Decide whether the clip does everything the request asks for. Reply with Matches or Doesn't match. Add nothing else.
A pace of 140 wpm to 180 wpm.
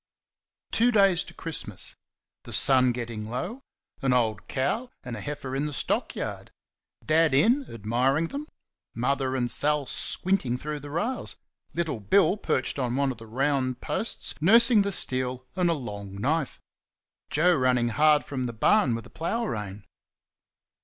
Matches